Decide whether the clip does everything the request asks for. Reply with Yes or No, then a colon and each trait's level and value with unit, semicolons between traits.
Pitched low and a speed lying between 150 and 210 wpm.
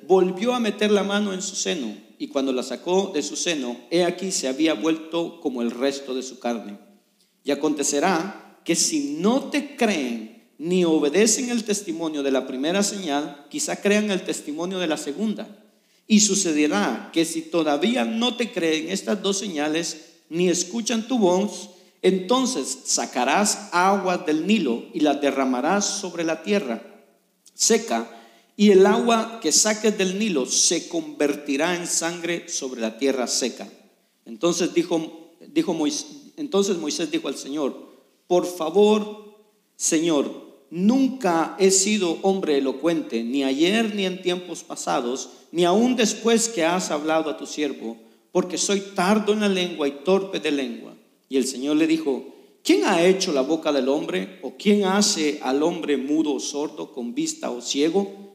No: medium, 175 Hz; average, 160 wpm